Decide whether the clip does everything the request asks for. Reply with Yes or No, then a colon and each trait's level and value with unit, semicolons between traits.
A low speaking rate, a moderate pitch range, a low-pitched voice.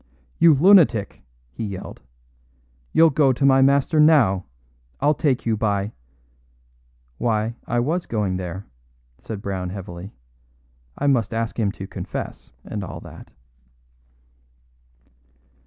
No: slow, 125 wpm; wide, 6.4 semitones; low, 110 Hz